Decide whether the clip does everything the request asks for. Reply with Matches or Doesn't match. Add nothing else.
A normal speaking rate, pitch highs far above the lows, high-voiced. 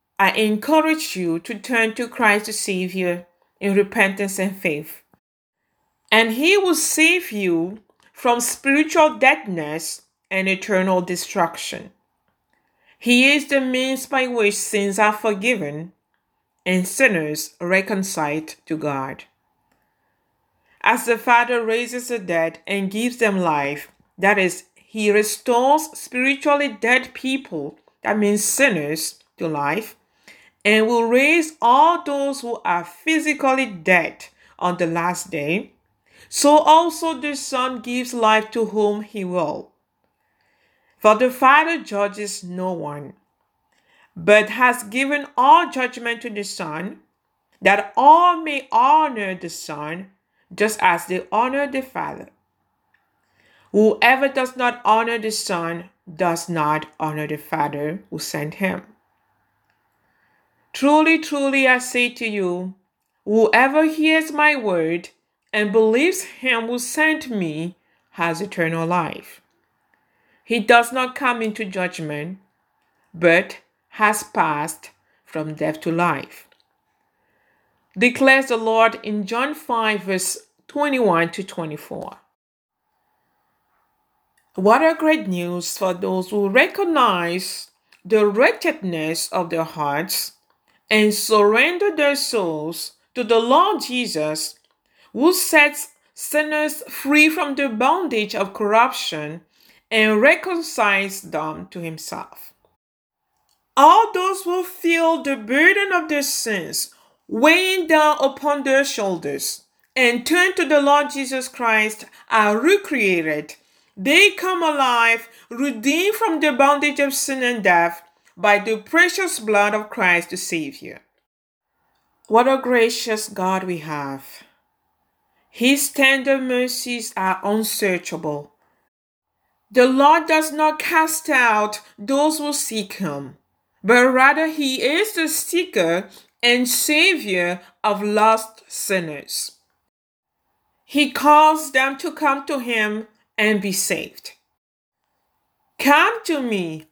Doesn't match